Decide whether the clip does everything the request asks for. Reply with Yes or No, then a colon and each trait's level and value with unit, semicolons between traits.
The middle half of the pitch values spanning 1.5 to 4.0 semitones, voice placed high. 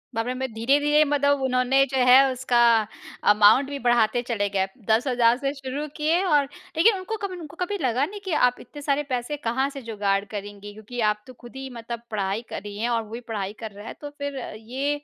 No: average, 4.4 semitones; very high, 250 Hz